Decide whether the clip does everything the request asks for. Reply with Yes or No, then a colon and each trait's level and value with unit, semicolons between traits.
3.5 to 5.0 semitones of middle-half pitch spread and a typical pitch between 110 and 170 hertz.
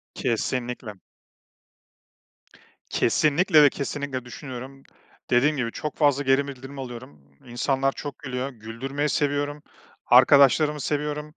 No: narrow, 2.6 semitones; low, 135 Hz